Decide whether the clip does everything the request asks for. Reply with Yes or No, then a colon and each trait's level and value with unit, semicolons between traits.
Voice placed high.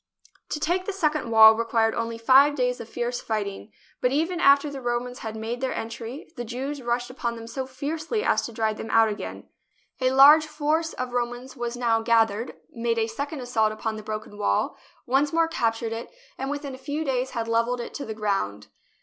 Yes: high, 245 Hz